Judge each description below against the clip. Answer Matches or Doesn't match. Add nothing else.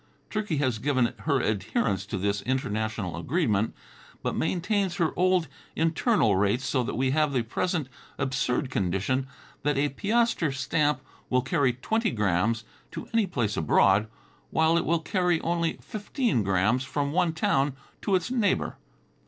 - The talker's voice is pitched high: Doesn't match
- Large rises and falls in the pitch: Matches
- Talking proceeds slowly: Doesn't match